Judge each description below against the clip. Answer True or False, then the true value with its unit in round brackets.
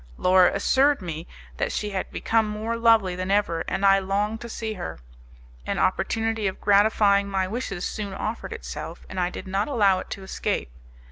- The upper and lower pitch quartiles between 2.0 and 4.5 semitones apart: True (2.7 semitones)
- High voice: True (200 Hz)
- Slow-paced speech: False (185 wpm)